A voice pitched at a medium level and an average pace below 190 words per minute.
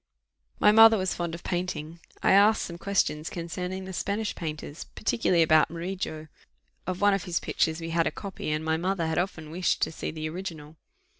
No: medium, 170 Hz; average, 195 wpm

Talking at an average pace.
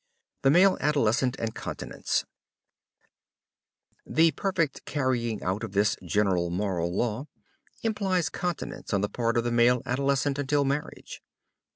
No: slow, 130 wpm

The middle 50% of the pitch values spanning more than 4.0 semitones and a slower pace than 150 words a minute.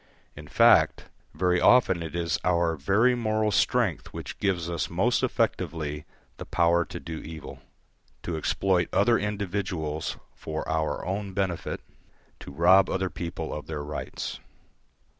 No: average, 3.5 semitones; average, 140 wpm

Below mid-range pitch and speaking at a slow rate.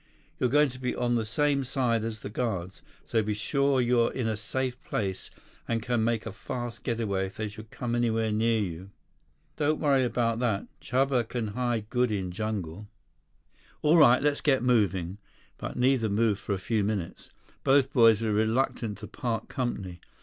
No: low, 115 Hz; average, 180 wpm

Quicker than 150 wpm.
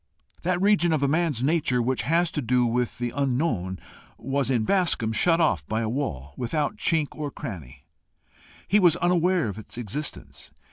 Yes: average, 175 wpm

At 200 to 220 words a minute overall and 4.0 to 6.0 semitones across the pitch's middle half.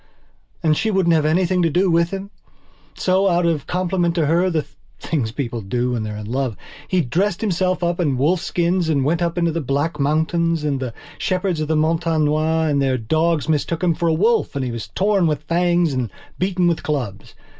No: fast, 205 wpm; average, 3.5 semitones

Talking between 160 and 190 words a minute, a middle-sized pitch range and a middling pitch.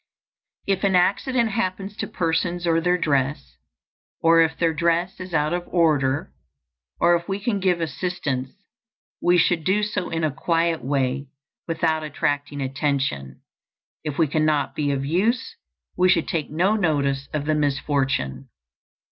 No: average, 145 wpm; average, 3.9 semitones; medium, 165 Hz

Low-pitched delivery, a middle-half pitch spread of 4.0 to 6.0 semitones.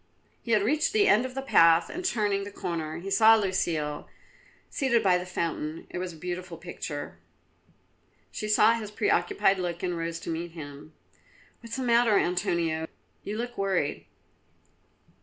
No: medium, 185 Hz; average, 5.2 semitones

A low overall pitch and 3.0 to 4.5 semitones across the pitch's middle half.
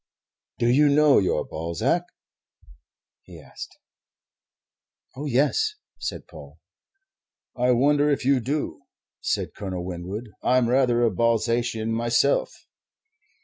Yes: low, 120 Hz; average, 3.9 semitones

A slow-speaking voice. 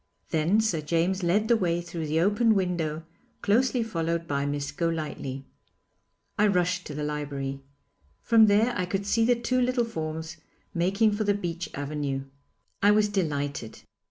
No: average, 155 wpm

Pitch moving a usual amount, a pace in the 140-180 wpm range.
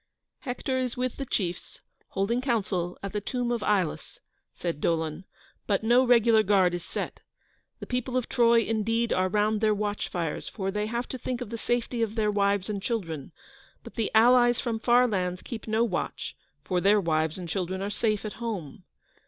No: average, 4.0 semitones; average, 190 wpm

